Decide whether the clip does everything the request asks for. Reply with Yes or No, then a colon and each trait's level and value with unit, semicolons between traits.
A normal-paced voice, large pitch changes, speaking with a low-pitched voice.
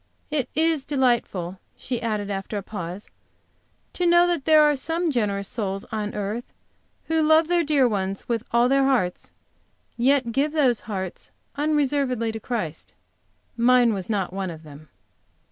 No: average, 155 wpm; wide, 6.5 semitones; high, 235 Hz